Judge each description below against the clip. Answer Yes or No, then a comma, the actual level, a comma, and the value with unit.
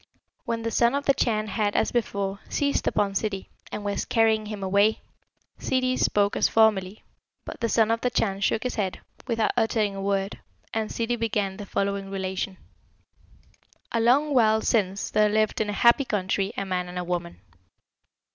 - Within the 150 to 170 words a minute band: No, average, 180 wpm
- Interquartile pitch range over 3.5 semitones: No, narrow, 2.6 semitones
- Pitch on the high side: Yes, high, 210 Hz